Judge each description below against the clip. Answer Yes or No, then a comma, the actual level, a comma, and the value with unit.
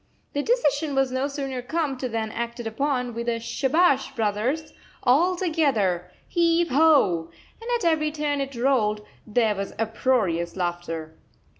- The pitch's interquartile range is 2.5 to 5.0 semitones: No, wide, 5.5 semitones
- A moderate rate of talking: Yes, average, 145 wpm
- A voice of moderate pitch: No, very high, 260 Hz